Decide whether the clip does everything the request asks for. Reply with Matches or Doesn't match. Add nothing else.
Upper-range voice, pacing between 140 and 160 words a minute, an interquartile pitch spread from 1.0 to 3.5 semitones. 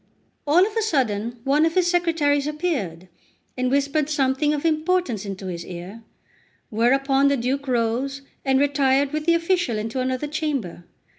Doesn't match